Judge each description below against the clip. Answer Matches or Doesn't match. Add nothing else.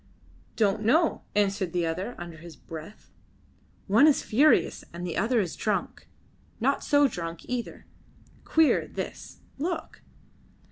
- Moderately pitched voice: Doesn't match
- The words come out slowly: Matches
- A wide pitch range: Matches